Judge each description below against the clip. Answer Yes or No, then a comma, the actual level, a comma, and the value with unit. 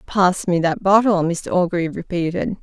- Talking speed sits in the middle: Yes, average, 160 wpm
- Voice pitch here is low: No, medium, 180 Hz